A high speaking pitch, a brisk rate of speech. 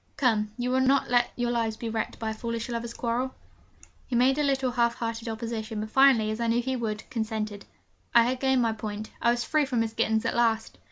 Yes: high, 235 Hz; fast, 230 wpm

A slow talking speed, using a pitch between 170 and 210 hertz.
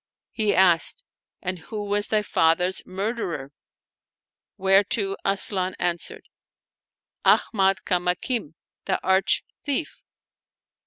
Yes: slow, 100 wpm; high, 190 Hz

